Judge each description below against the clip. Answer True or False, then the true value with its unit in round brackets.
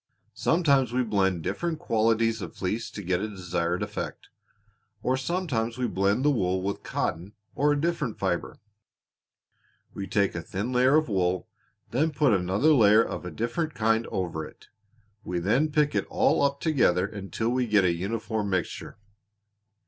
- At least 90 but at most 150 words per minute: False (165 wpm)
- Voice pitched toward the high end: False (110 Hz)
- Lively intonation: True (6.2 semitones)